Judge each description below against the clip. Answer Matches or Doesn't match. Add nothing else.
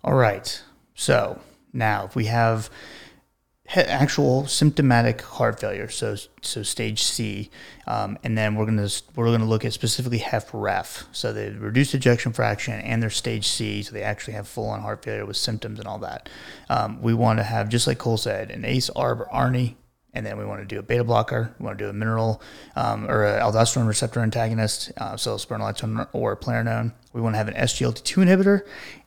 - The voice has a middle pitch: Doesn't match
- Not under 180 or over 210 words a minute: Matches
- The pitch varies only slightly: Matches